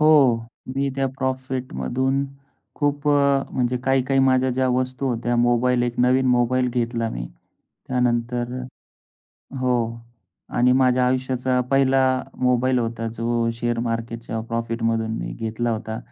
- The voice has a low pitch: Yes, low, 125 Hz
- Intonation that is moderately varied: No, narrow, 1.9 semitones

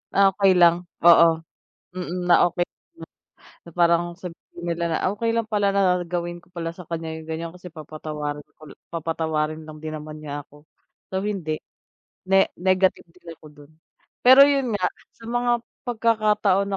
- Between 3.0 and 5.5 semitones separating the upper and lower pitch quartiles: Yes, average, 3.4 semitones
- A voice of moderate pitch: Yes, medium, 175 Hz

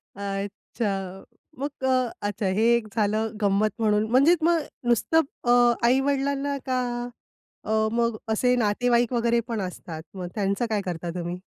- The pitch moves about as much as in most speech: Yes, average, 3.8 semitones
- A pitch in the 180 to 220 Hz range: No, high, 230 Hz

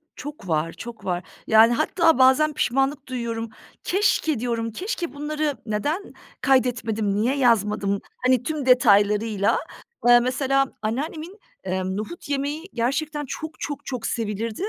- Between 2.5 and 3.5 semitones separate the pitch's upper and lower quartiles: No, average, 5.2 semitones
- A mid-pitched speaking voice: No, very high, 250 Hz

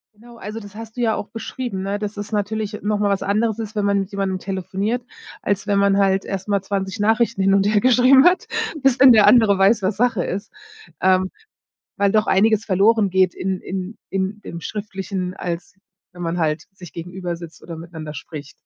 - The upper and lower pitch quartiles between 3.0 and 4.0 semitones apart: No, narrow, 2.4 semitones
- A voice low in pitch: No, high, 200 Hz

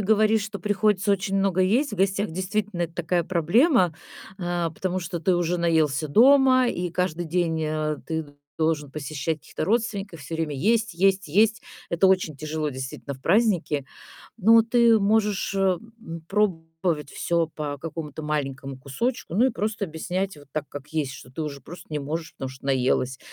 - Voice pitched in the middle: Yes, medium, 175 Hz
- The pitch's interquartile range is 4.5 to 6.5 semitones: Yes, average, 4.8 semitones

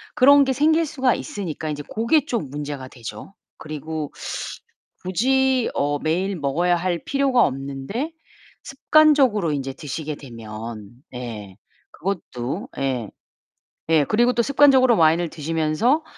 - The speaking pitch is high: No, medium, 165 Hz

